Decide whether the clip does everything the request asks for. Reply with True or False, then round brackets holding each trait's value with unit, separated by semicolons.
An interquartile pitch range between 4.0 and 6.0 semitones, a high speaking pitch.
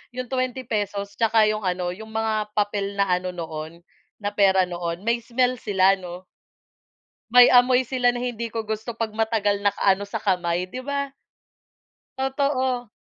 True (4.3 semitones; 215 Hz)